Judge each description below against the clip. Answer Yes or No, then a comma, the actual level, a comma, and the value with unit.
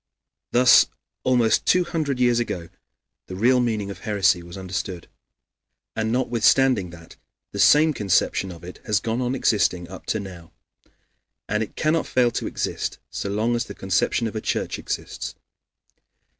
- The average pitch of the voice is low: Yes, low, 110 Hz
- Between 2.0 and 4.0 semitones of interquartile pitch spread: No, average, 4.7 semitones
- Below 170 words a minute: Yes, average, 155 wpm